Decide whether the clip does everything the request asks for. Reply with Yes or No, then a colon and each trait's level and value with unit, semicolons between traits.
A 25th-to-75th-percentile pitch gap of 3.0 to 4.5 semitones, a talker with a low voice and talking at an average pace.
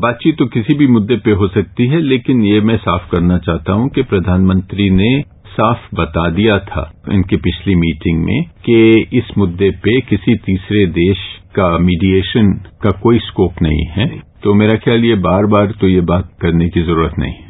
Yes: average, 4.2 semitones; low, 100 Hz; average, 190 wpm